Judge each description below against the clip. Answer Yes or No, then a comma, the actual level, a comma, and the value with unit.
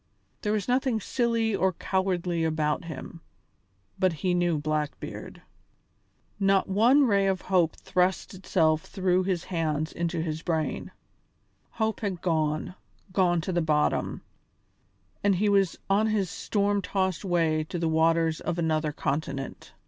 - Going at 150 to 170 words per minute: No, average, 140 wpm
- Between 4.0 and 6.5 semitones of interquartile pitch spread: No, average, 3.5 semitones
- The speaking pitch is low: No, medium, 180 Hz